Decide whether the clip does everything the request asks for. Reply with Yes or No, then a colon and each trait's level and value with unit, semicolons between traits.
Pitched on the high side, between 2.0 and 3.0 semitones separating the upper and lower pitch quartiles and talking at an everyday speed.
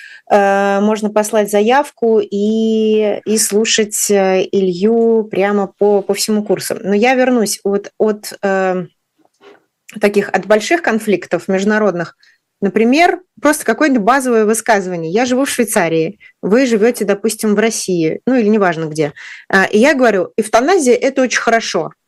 Yes: high, 215 Hz; narrow, 2.6 semitones; average, 130 wpm